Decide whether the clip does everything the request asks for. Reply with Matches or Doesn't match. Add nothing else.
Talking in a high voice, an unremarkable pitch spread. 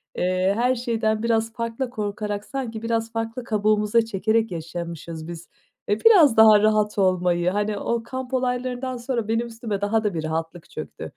Matches